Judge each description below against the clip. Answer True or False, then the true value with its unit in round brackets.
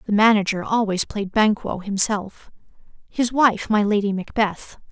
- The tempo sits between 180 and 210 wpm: False (135 wpm)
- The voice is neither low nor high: False (210 Hz)